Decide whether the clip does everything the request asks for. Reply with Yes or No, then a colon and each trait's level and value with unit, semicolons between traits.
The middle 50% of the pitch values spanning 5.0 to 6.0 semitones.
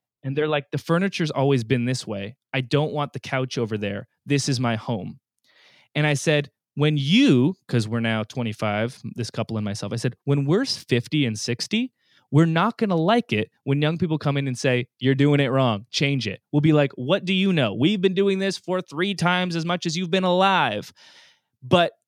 Yes: wide, 5.5 semitones